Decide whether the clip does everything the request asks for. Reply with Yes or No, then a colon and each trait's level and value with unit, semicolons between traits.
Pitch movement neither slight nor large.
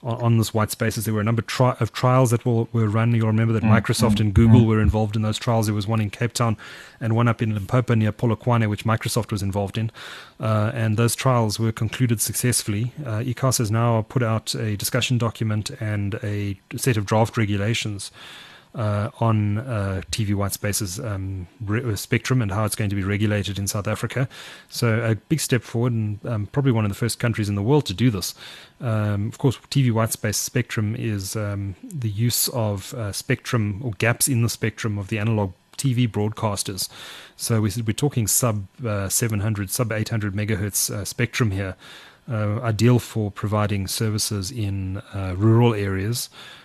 No: narrow, 2.2 semitones